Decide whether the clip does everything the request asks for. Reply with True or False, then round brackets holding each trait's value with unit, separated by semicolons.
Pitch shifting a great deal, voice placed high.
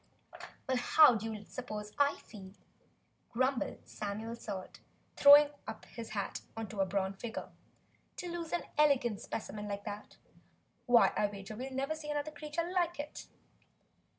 True (5.9 semitones; 235 Hz)